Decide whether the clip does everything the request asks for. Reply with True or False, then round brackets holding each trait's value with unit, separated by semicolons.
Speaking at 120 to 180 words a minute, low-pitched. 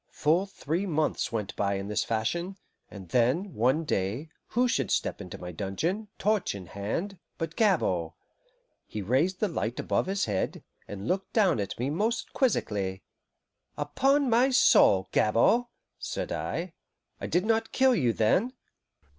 False (155 wpm; 150 Hz)